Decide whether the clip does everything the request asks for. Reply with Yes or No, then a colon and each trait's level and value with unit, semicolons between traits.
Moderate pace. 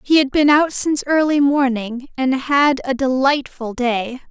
Yes: average, 165 wpm